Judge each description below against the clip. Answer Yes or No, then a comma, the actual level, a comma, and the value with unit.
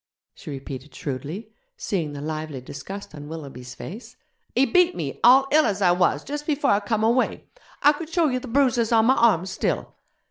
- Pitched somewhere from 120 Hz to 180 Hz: No, high, 205 Hz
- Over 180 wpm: Yes, average, 190 wpm